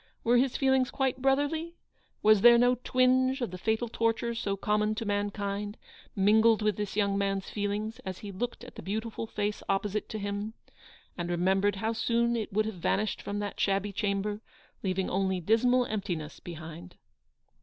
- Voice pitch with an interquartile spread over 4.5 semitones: No, average, 3.0 semitones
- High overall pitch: Yes, high, 210 Hz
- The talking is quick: No, average, 175 wpm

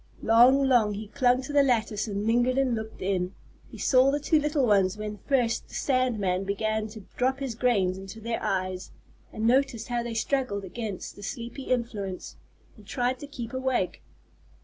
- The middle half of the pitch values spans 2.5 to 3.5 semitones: No, average, 4.0 semitones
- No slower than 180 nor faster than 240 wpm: Yes, average, 185 wpm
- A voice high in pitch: Yes, high, 230 Hz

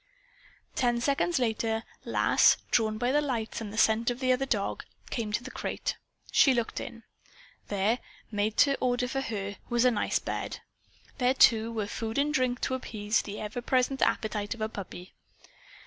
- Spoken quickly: No, average, 180 wpm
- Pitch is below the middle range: No, high, 230 Hz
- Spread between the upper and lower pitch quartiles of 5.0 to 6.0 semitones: No, average, 2.8 semitones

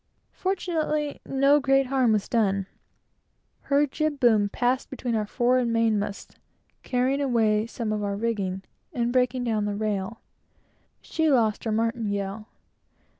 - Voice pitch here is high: Yes, high, 230 Hz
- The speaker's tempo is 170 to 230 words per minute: No, average, 140 wpm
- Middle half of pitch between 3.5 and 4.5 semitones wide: Yes, average, 4.0 semitones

